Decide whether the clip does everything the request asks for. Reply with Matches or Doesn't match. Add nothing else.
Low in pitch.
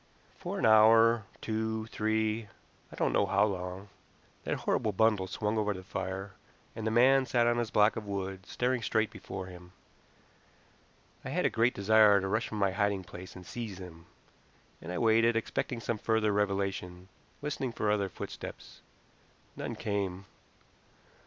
Matches